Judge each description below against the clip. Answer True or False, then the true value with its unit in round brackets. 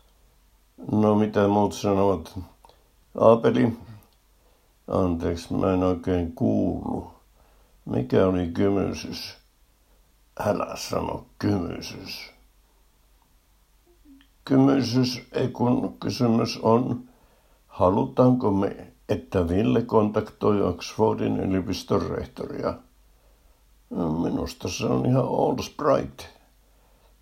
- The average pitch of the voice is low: True (100 Hz)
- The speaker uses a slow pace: True (75 wpm)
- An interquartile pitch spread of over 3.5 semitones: True (5.0 semitones)